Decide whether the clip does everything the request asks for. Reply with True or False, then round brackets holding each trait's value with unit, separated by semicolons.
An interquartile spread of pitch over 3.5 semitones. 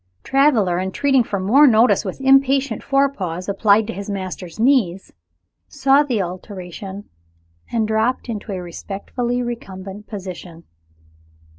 True (5.3 semitones)